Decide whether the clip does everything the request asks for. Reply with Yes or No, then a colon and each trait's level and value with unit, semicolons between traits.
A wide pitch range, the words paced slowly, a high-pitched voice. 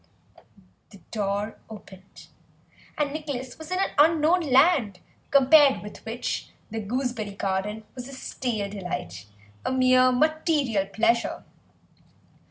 Yes: wide, 5.8 semitones; slow, 115 wpm; very high, 250 Hz